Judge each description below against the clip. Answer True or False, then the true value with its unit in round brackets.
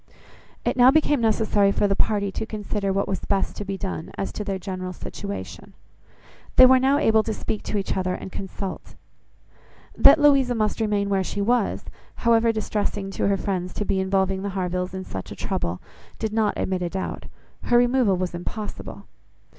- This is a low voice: False (200 Hz)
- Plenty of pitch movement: False (2.6 semitones)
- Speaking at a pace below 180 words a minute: False (185 wpm)